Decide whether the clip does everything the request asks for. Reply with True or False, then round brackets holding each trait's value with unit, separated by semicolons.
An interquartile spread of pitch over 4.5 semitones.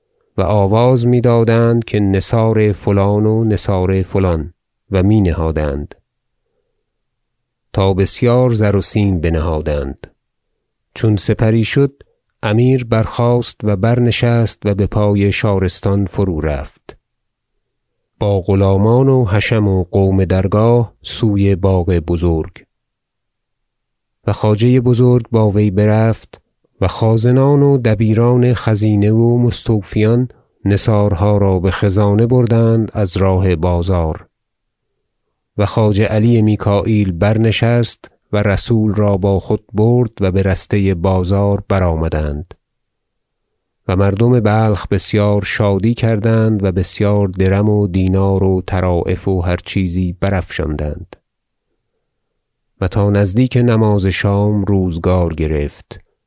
False (3.0 semitones)